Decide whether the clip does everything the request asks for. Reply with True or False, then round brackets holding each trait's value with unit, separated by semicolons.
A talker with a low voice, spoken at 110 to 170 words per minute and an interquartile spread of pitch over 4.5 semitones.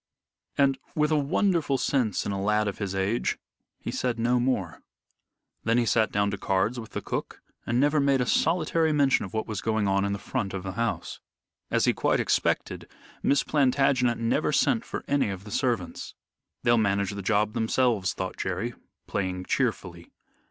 False (115 Hz; 185 wpm; 5.0 semitones)